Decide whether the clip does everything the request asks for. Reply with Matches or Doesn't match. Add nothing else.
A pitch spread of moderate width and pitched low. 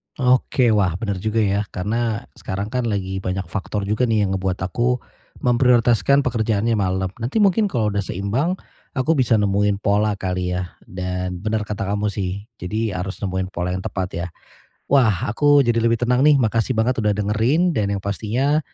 Matches